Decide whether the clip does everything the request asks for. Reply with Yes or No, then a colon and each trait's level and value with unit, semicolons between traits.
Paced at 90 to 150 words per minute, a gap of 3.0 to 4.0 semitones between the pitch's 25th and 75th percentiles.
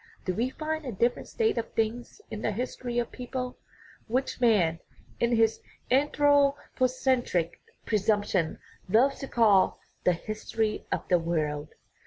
No: average, 140 wpm; average, 4.4 semitones